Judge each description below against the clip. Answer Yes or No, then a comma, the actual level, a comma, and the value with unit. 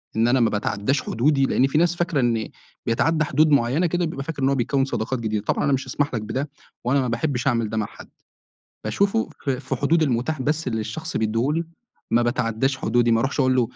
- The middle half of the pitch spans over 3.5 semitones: Yes, average, 4.0 semitones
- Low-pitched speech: Yes, low, 130 Hz